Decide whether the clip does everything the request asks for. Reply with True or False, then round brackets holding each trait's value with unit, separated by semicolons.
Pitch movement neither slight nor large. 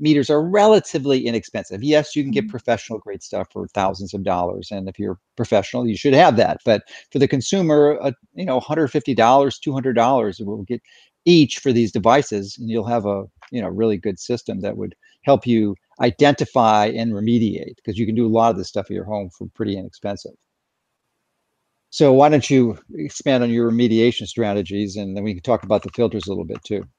True (4.8 semitones)